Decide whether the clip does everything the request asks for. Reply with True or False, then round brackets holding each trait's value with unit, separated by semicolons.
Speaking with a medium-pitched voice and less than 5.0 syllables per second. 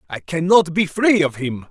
True (170 Hz; 4.6 syllables/s)